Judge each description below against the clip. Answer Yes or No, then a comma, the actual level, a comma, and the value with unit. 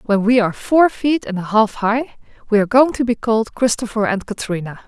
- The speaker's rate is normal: No, fast, 220 wpm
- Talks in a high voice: Yes, high, 225 Hz